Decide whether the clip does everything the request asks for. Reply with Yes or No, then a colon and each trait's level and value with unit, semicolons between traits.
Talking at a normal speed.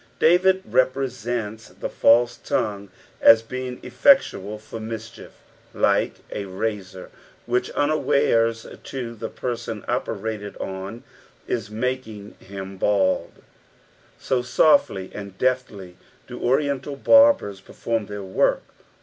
No: slow, 105 wpm